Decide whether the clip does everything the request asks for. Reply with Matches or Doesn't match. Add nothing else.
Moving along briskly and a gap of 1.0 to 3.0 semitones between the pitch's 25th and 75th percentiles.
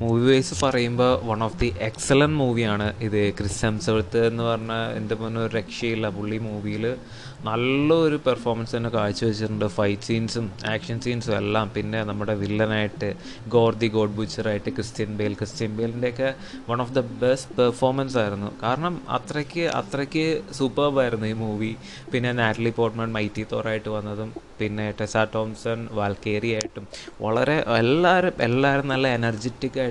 Matches